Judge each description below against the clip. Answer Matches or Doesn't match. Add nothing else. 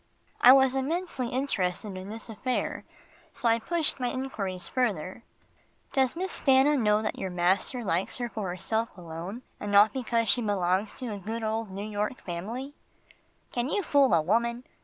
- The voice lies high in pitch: Matches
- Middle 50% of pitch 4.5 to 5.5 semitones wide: Matches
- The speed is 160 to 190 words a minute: Matches